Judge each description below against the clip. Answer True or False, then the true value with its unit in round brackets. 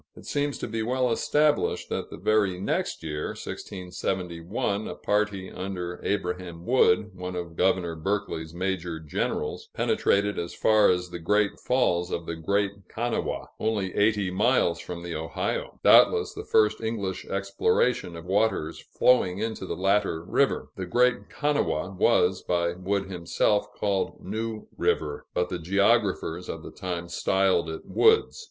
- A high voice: False (95 Hz)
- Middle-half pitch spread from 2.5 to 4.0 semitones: True (3.4 semitones)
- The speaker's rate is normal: True (150 wpm)